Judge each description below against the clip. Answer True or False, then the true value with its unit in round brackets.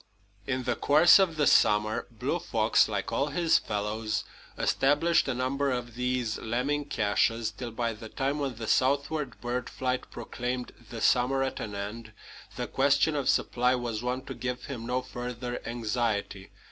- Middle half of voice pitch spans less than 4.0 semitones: True (3.0 semitones)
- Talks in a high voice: False (125 Hz)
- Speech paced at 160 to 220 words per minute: True (165 wpm)